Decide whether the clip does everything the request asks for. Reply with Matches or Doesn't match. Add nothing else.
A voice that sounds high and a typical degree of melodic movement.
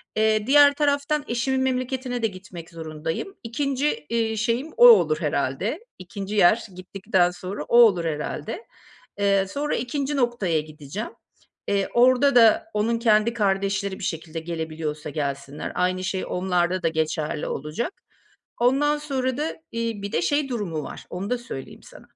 Doesn't match